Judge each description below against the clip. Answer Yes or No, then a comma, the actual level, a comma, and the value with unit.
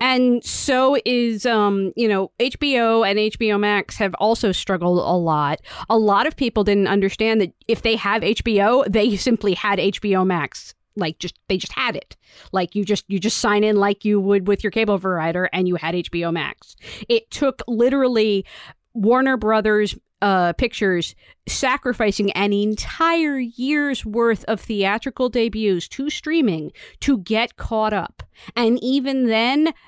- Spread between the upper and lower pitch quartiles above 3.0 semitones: Yes, average, 3.6 semitones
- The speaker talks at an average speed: Yes, average, 160 wpm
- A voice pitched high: Yes, high, 215 Hz